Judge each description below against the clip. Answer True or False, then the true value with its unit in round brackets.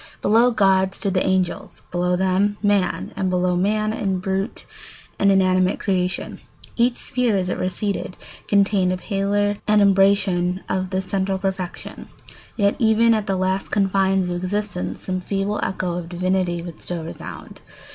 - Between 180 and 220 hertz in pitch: True (190 Hz)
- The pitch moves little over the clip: True (1.8 semitones)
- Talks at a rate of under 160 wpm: True (150 wpm)